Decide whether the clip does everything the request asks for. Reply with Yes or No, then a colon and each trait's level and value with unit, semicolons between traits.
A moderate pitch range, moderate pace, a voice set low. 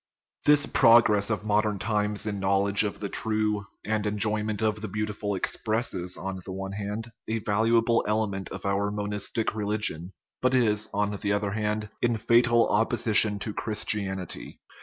No: narrow, 1.4 semitones; average, 160 wpm; low, 105 Hz